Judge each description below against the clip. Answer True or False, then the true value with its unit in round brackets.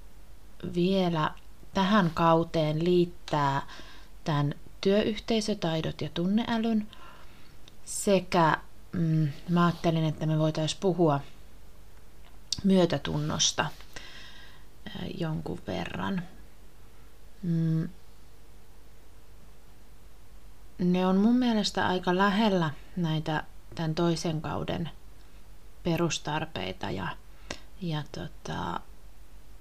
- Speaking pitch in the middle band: True (165 Hz)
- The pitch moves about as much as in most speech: True (3.3 semitones)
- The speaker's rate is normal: False (70 wpm)